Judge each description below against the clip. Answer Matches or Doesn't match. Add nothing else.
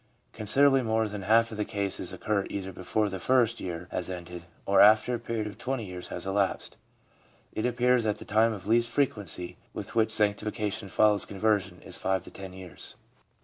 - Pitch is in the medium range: Doesn't match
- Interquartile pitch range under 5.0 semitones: Matches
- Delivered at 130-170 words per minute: Doesn't match